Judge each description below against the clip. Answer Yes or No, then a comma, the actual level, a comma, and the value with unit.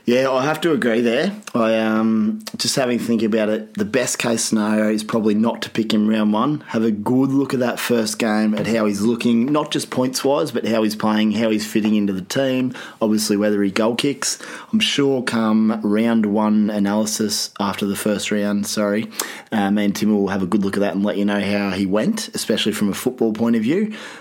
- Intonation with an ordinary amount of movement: No, narrow, 2.1 semitones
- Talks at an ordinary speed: No, fast, 230 wpm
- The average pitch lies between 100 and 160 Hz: Yes, low, 110 Hz